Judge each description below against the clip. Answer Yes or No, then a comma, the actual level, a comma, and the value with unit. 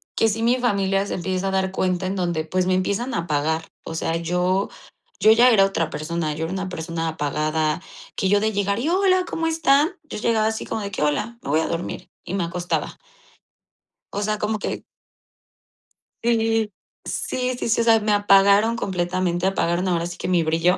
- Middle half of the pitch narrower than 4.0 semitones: No, average, 4.3 semitones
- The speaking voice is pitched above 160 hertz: Yes, high, 190 Hz